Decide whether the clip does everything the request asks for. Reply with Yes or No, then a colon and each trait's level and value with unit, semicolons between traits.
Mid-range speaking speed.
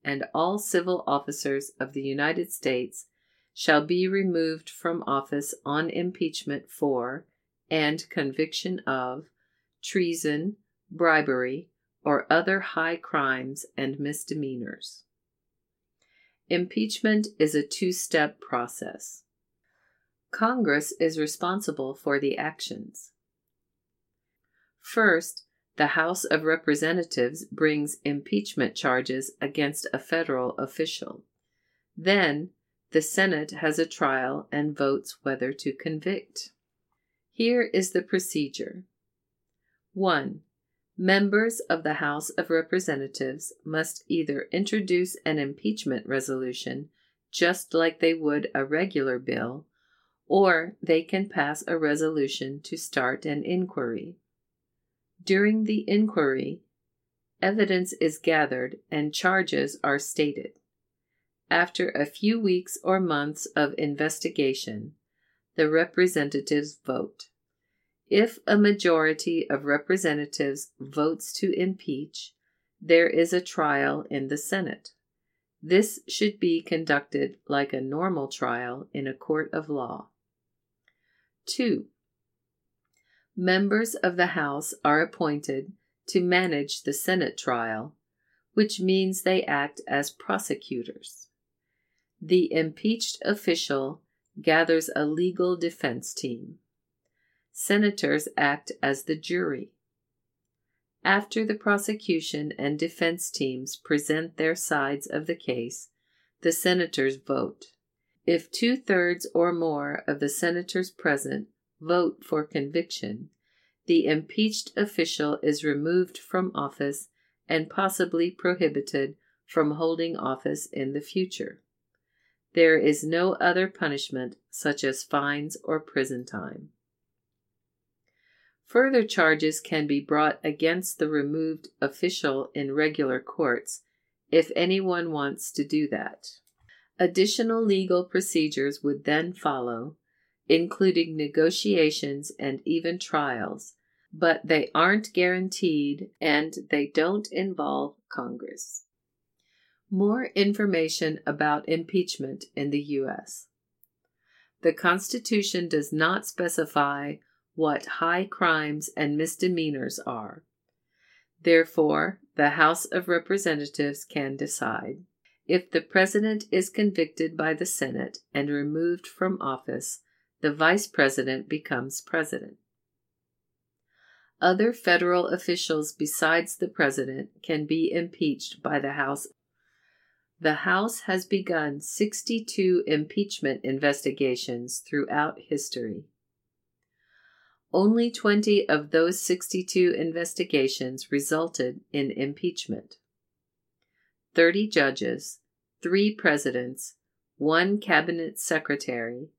No: slow, 105 wpm